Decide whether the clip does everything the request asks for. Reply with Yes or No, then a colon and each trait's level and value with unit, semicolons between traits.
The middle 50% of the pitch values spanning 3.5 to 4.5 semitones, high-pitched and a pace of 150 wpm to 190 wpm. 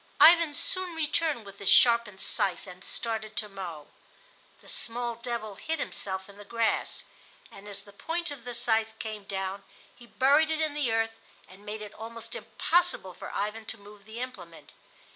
Yes: average, 4.0 semitones; high, 225 Hz; average, 180 wpm